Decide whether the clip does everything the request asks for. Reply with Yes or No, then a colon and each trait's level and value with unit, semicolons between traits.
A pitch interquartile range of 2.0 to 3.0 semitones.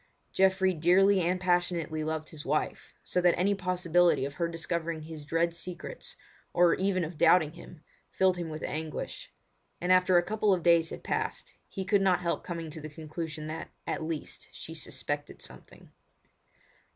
Yes: narrow, 2.5 semitones